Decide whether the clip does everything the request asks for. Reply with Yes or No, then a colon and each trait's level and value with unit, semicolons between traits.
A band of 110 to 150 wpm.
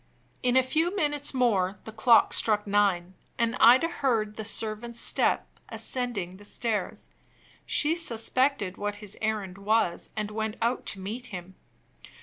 Yes: average, 145 wpm